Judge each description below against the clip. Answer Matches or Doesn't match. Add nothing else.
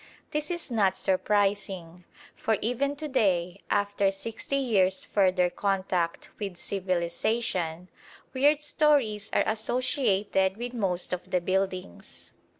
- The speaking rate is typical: Doesn't match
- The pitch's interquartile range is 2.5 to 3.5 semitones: Doesn't match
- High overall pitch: Matches